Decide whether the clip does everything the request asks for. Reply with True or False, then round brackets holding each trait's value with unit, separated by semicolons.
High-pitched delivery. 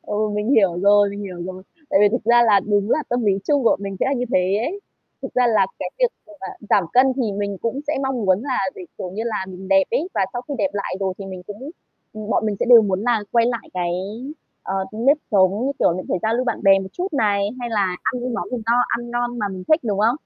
True (215 Hz)